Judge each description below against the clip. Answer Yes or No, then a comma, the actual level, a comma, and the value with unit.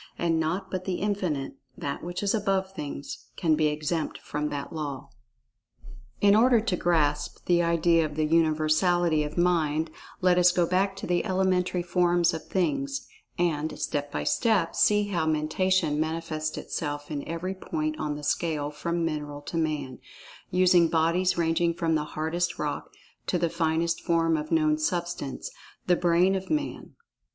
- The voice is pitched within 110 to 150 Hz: No, medium, 165 Hz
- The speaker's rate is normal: Yes, average, 155 wpm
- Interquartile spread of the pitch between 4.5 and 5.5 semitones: No, average, 2.7 semitones